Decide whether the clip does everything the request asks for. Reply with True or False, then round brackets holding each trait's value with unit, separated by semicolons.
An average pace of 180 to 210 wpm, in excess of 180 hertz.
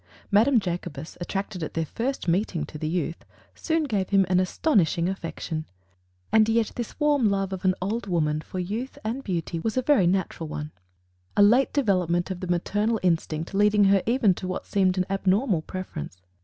True (185 wpm; 190 Hz)